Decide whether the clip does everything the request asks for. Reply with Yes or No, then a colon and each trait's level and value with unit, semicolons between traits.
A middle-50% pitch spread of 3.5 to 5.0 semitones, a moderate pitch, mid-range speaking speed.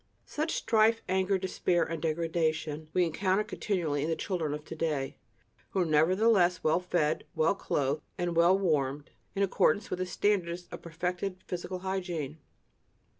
No: average, 3.1 semitones; medium, 175 Hz; average, 155 wpm